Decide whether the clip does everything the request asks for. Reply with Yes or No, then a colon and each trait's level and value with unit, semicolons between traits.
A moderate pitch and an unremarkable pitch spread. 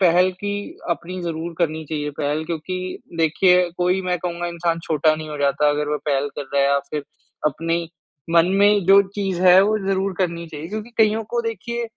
Yes: medium, 170 Hz; average, 3.4 semitones